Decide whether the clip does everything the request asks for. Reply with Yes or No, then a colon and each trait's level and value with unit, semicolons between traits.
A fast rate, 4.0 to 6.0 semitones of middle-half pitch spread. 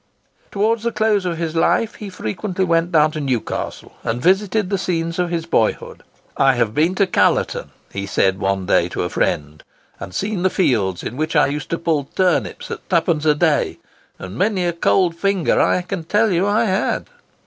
No: average, 195 wpm; wide, 5.4 semitones